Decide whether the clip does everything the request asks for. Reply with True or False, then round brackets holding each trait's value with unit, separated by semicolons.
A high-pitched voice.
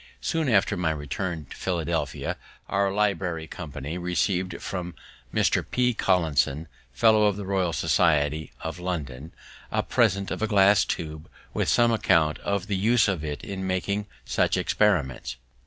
False (90 Hz)